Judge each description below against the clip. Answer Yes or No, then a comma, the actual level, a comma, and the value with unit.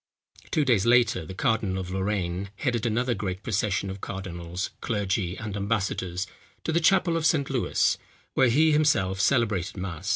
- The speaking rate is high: No, average, 160 wpm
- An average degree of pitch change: Yes, average, 4.7 semitones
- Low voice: Yes, low, 105 Hz